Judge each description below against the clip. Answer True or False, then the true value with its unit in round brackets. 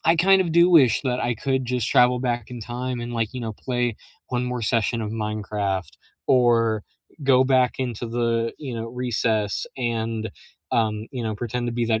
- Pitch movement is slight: True (2.1 semitones)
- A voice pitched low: True (120 Hz)